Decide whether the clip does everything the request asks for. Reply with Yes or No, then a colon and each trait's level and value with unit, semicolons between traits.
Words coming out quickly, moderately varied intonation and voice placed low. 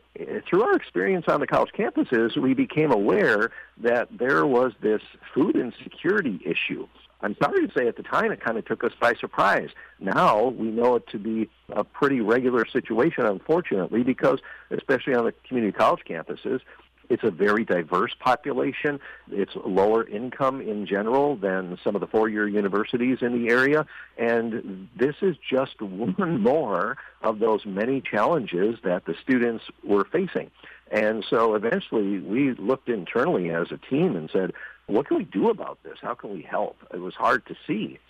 No: average, 175 wpm; average, 4.0 semitones; low, 120 Hz